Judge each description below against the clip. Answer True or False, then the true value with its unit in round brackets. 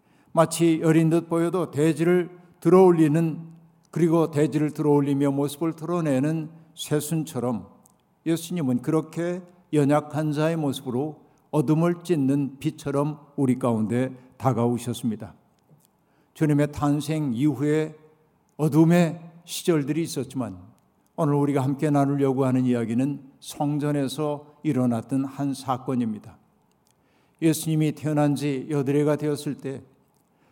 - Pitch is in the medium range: True (150 Hz)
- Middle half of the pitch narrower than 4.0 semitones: True (2.7 semitones)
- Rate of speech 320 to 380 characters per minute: False (275 characters per minute)